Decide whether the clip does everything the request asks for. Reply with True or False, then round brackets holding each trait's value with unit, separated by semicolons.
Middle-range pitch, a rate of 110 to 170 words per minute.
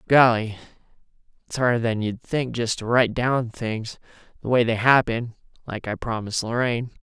False (115 Hz; 160 wpm)